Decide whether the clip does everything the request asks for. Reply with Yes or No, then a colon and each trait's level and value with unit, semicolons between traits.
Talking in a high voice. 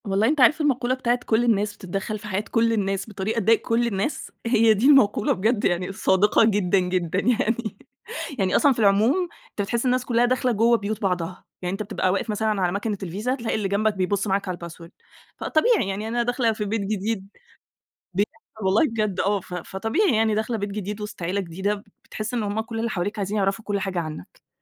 Yes: high, 210 Hz